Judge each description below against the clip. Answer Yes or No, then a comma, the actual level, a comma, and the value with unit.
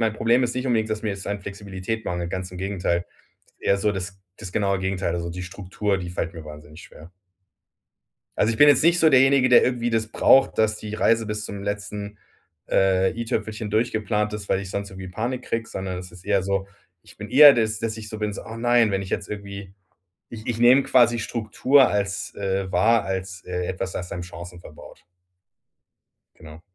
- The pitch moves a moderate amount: Yes, average, 3.2 semitones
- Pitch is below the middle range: Yes, low, 100 Hz